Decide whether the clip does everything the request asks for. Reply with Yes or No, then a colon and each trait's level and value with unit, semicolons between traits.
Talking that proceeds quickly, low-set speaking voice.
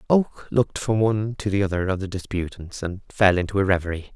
Yes: fast, 215 wpm; low, 100 Hz